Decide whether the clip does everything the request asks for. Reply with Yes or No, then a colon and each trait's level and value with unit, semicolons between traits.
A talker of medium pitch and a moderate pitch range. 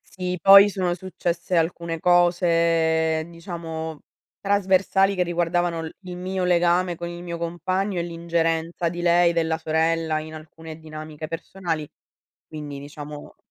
No: medium, 170 Hz; narrow, 1.7 semitones